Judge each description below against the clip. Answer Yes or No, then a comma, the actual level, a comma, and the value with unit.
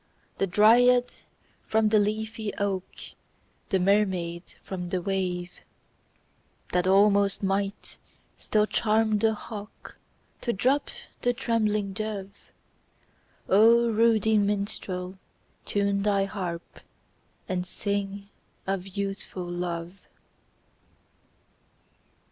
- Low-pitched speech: No, high, 200 Hz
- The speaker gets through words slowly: Yes, slow, 90 wpm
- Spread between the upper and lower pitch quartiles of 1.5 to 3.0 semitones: Yes, narrow, 2.4 semitones